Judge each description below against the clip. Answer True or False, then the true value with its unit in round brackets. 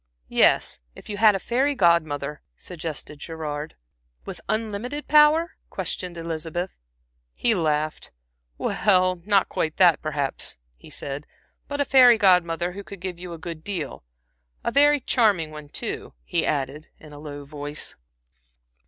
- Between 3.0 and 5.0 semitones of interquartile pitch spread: False (5.4 semitones)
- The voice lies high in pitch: False (175 Hz)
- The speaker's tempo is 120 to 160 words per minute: True (145 wpm)